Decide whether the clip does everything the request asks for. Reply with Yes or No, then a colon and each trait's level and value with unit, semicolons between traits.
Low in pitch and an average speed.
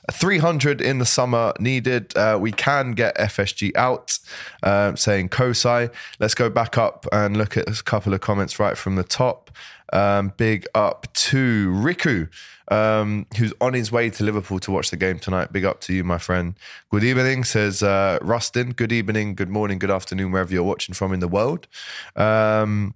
Yes: low, 105 Hz; average, 185 wpm